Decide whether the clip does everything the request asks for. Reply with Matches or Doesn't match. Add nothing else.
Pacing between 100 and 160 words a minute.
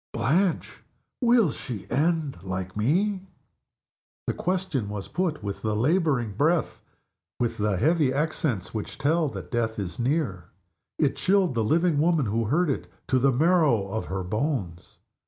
Matches